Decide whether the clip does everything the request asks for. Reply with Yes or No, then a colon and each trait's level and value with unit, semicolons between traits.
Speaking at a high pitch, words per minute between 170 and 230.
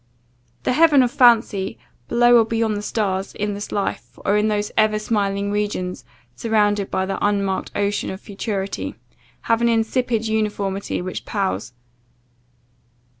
No: high, 210 Hz; average, 140 wpm